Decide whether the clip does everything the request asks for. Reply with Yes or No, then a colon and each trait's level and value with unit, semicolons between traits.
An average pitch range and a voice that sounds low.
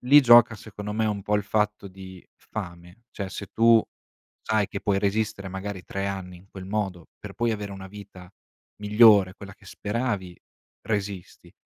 No: narrow, 2.1 semitones; low, 100 Hz